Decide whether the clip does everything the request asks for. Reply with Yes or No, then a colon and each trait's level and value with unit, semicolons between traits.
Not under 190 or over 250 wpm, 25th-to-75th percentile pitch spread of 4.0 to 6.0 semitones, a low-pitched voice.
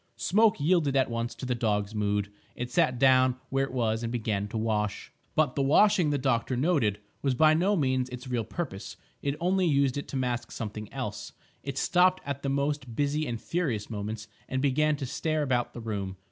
Yes: average, 200 wpm; average, 4.4 semitones; low, 130 Hz